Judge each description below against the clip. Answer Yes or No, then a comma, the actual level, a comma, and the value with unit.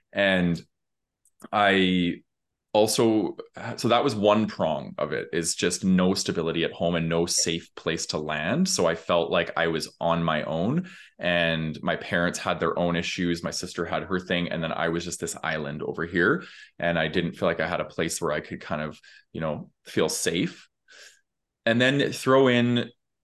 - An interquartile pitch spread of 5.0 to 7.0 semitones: Yes, average, 5.3 semitones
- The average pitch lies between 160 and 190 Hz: No, very low, 90 Hz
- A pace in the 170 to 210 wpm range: Yes, average, 190 wpm